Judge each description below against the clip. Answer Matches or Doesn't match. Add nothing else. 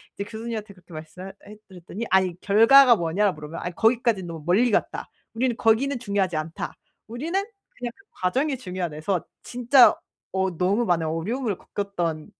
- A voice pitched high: Matches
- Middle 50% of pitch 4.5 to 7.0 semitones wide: Matches